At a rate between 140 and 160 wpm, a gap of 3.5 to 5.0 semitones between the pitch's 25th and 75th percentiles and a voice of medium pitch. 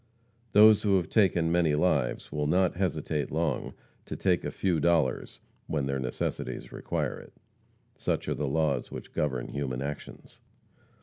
No: average, 150 wpm; average, 4.0 semitones; very low, 80 Hz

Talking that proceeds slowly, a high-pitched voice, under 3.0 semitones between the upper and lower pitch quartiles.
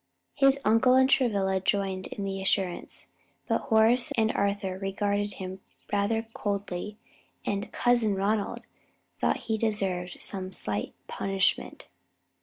Yes: slow, 120 wpm; high, 200 Hz; narrow, 2.5 semitones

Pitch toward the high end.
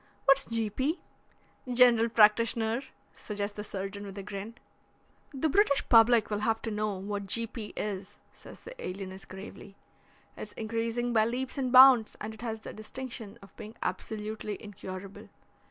Yes: high, 220 Hz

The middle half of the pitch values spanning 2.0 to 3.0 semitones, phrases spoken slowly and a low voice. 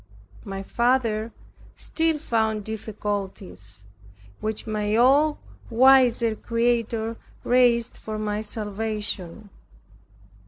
No: narrow, 2.4 semitones; slow, 80 wpm; high, 220 Hz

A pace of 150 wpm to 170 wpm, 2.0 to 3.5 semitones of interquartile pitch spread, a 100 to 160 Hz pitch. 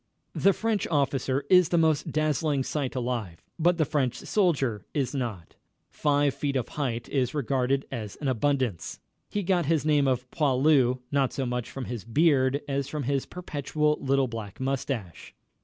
Yes: average, 165 wpm; average, 3.1 semitones; medium, 140 Hz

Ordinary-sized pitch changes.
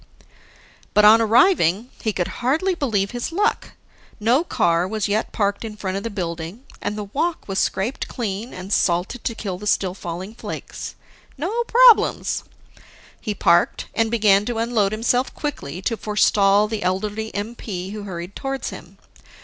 Yes: average, 3.6 semitones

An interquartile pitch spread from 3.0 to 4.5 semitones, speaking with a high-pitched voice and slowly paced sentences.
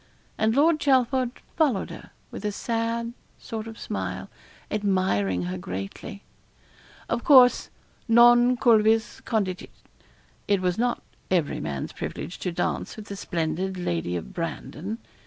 No: wide, 5.4 semitones; high, 210 Hz; slow, 130 wpm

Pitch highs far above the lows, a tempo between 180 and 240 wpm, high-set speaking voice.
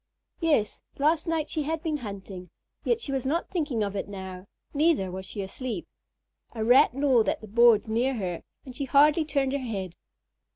Yes: wide, 6.7 semitones; average, 190 wpm; very high, 255 Hz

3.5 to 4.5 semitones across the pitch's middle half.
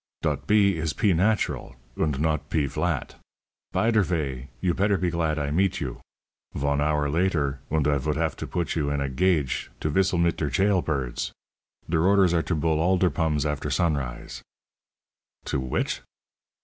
Yes: average, 3.9 semitones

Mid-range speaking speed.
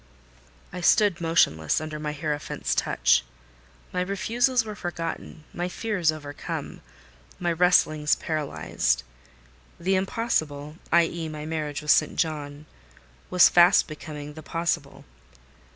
No: slow, 100 wpm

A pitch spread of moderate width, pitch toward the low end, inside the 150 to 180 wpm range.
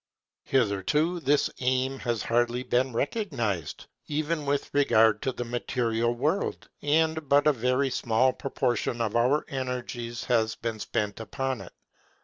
No: average, 3.4 semitones; low, 125 Hz; slow, 135 wpm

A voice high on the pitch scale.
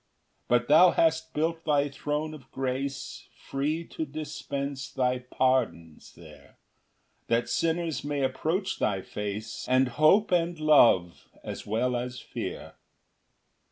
No: medium, 140 Hz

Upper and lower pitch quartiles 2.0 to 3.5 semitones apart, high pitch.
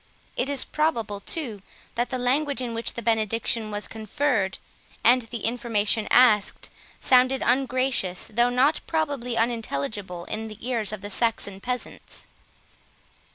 Yes: average, 3.1 semitones; high, 235 Hz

